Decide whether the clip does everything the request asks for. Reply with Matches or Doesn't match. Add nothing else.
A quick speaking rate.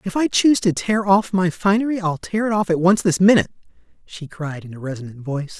Matches